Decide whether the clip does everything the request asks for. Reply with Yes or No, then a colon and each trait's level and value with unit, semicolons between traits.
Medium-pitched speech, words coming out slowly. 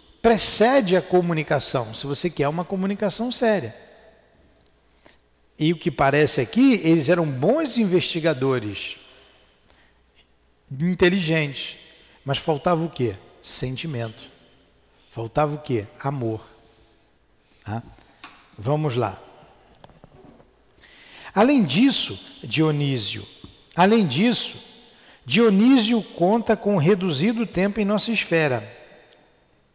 Yes: medium, 160 Hz; slow, 90 wpm